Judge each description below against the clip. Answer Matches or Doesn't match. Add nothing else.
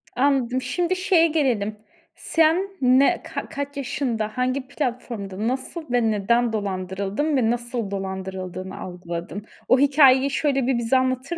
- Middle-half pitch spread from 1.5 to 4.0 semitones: Doesn't match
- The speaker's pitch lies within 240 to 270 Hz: Matches